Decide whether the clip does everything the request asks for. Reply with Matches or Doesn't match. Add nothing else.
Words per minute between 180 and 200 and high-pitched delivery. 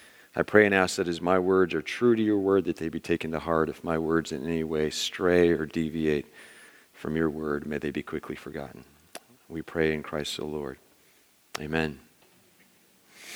Doesn't match